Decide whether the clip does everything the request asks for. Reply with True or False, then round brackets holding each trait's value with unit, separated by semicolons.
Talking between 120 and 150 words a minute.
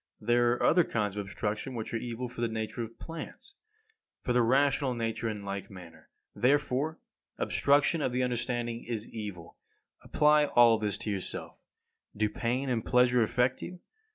False (165 wpm)